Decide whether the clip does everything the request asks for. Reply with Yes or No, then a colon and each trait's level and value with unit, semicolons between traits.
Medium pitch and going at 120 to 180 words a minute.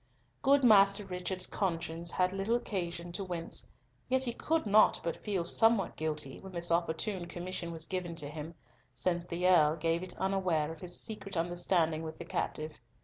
Yes: medium, 175 Hz; average, 175 wpm